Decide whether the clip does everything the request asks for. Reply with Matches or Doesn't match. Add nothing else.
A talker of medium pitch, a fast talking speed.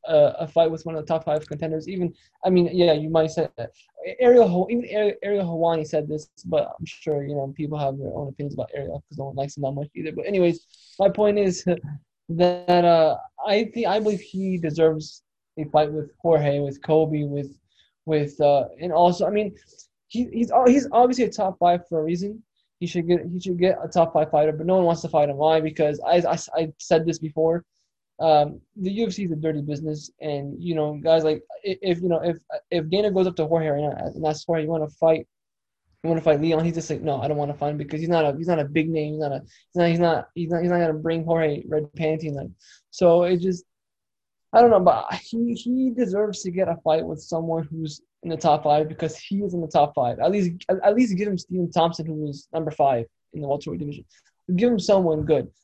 Matches